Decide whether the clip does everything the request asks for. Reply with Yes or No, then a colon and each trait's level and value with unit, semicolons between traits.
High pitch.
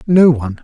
No: medium, 140 Hz